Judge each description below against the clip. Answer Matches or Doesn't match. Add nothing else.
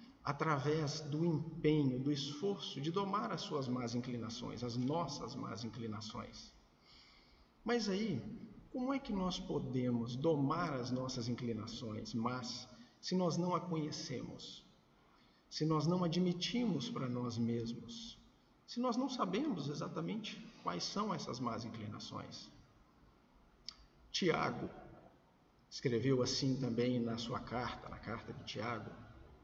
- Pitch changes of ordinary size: Doesn't match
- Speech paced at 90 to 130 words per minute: Matches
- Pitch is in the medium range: Matches